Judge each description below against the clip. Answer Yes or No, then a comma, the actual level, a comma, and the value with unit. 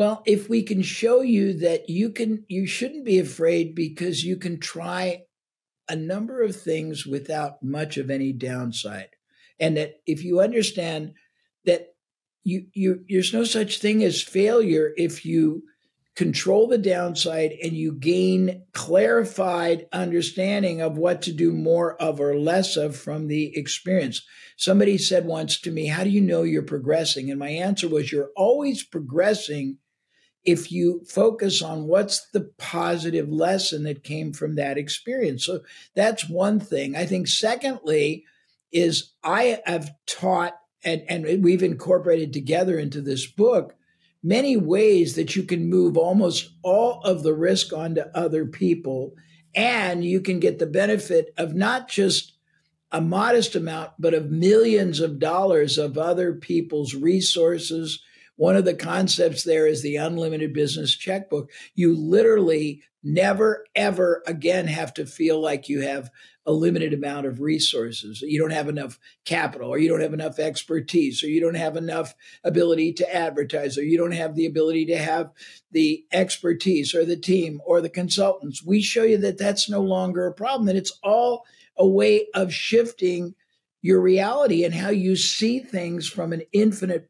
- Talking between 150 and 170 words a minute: Yes, average, 160 wpm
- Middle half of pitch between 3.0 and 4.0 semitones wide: Yes, average, 3.3 semitones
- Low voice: No, medium, 170 Hz